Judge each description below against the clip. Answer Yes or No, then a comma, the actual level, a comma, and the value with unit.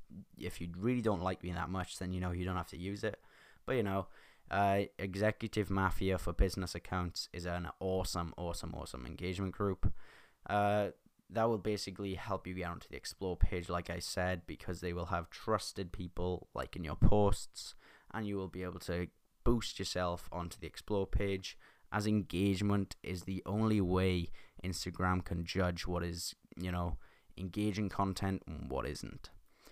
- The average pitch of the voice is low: Yes, very low, 90 Hz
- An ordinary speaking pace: Yes, average, 175 wpm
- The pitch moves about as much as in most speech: No, narrow, 2.2 semitones